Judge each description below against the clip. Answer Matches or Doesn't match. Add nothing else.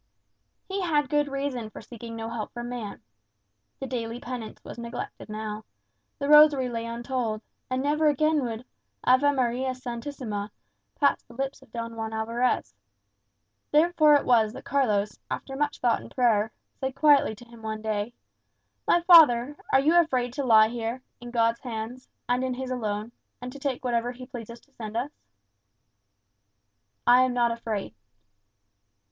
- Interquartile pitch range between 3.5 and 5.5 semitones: Doesn't match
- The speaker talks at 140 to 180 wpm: Matches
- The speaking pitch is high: Matches